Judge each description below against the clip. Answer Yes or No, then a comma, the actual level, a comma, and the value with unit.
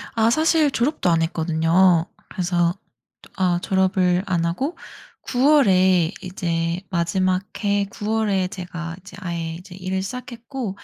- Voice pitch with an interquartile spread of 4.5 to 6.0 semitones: No, average, 3.4 semitones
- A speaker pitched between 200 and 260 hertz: No, medium, 185 Hz